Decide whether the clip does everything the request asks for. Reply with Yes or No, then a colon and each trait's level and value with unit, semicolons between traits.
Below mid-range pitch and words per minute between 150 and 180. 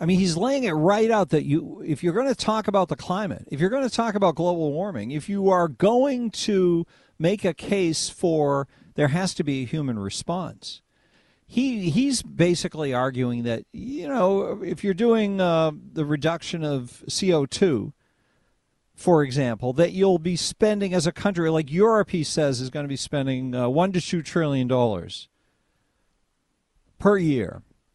No: medium, 170 Hz; average, 170 wpm